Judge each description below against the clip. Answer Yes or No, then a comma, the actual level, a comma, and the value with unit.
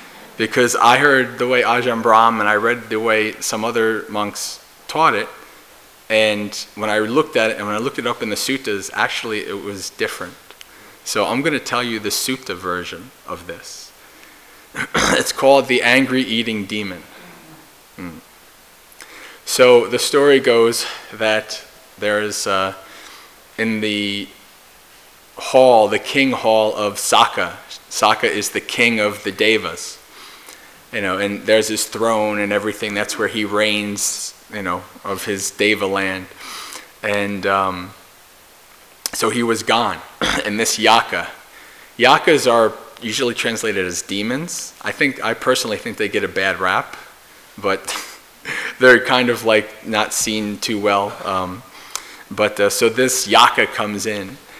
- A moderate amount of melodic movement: No, narrow, 2.1 semitones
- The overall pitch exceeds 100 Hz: Yes, low, 110 Hz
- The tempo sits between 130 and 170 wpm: Yes, average, 150 wpm